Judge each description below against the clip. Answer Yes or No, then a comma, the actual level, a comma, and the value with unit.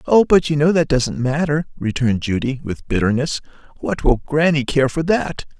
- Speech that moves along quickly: No, average, 180 wpm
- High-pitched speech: No, medium, 145 Hz